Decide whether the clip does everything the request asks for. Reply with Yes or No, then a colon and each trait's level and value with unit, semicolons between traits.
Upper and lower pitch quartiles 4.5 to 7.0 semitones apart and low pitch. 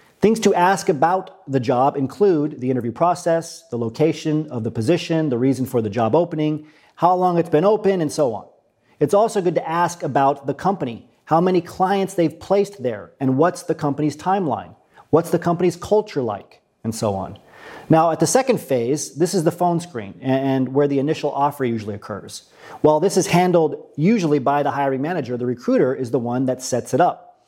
No: average, 4.9 semitones; medium, 155 Hz